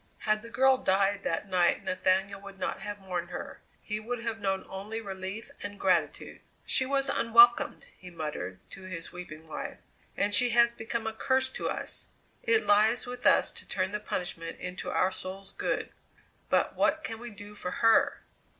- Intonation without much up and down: No, average, 3.8 semitones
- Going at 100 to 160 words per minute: No, average, 180 wpm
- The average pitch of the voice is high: Yes, high, 205 Hz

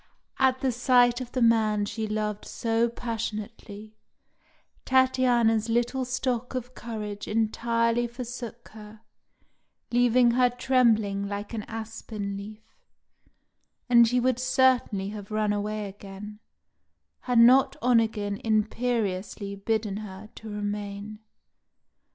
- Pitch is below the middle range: No, high, 225 Hz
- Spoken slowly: Yes, slow, 110 wpm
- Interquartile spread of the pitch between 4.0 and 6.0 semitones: No, narrow, 2.6 semitones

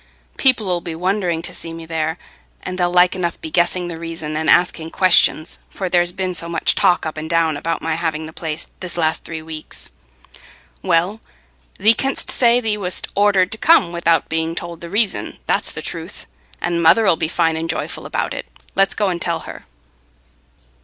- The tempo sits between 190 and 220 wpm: Yes, average, 195 wpm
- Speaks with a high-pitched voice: No, medium, 170 Hz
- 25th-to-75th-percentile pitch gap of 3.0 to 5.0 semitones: No, narrow, 2.4 semitones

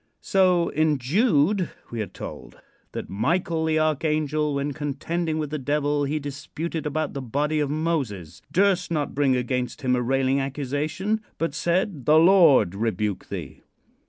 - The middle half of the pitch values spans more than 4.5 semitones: No, average, 3.3 semitones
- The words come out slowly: No, average, 155 wpm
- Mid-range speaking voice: Yes, medium, 150 Hz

